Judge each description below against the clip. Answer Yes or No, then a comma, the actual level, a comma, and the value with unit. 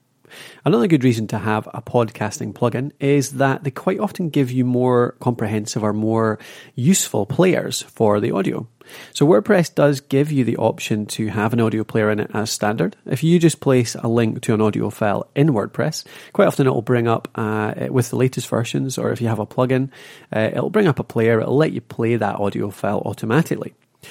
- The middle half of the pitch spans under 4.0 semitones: No, average, 4.3 semitones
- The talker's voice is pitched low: Yes, low, 120 Hz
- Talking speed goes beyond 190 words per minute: Yes, fast, 205 wpm